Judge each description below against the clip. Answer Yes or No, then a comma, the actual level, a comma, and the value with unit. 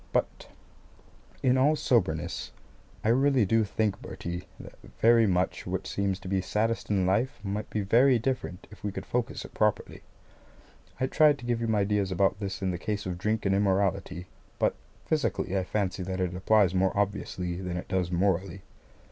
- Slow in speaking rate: No, average, 180 wpm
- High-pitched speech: No, low, 100 Hz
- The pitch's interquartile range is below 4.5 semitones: Yes, average, 3.3 semitones